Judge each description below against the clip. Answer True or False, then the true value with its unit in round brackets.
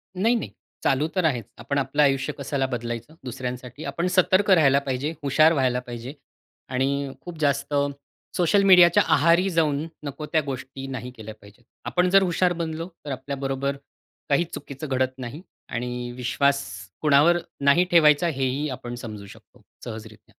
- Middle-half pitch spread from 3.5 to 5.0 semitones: True (4.1 semitones)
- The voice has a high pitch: False (140 Hz)